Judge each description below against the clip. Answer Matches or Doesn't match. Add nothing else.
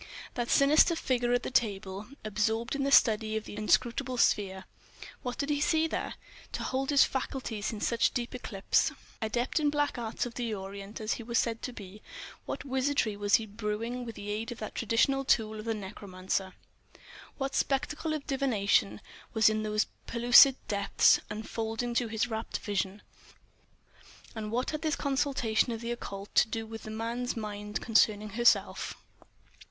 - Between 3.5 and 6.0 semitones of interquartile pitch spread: Doesn't match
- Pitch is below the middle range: Doesn't match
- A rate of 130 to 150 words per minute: Doesn't match